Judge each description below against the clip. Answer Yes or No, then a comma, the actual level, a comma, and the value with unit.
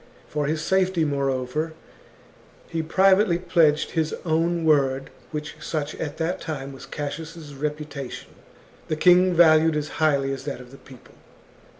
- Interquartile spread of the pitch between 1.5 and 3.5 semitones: Yes, narrow, 2.6 semitones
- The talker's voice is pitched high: No, medium, 155 Hz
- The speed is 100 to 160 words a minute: Yes, average, 140 wpm